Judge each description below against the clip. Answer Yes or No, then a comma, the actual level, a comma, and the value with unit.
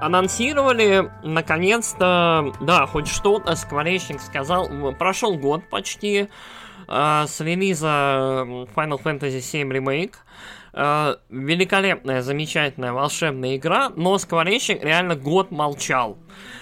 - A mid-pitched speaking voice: Yes, medium, 160 Hz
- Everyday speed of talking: No, slow, 100 wpm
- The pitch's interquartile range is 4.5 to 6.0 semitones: Yes, average, 5.1 semitones